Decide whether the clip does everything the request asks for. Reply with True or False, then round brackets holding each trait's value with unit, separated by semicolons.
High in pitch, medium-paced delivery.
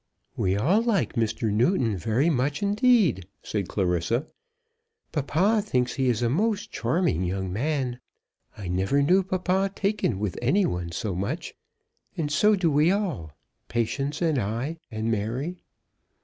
False (135 Hz; 145 wpm)